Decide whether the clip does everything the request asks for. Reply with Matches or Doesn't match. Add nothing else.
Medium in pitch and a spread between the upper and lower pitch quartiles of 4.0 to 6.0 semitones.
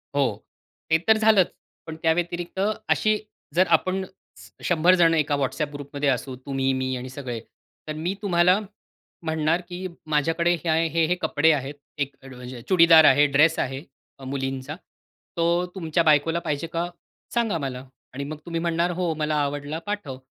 Doesn't match